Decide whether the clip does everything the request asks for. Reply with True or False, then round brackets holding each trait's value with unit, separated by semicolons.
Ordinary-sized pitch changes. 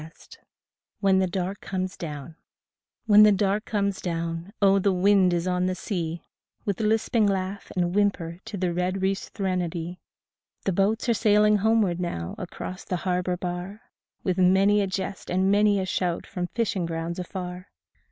False (2.2 semitones)